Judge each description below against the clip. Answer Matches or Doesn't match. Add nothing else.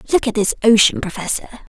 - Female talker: Matches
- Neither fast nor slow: Matches